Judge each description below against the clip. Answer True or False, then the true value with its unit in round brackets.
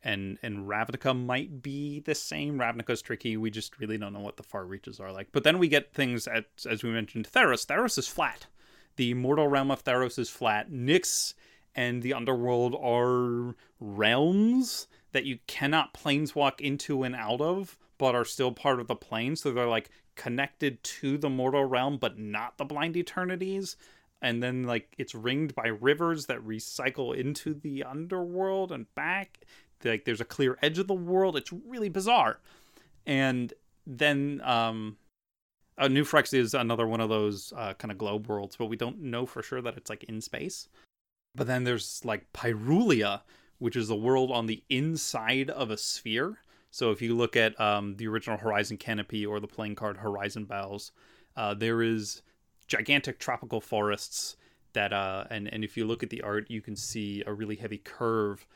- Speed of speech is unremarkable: True (185 wpm)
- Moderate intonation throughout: True (4.5 semitones)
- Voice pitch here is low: True (120 Hz)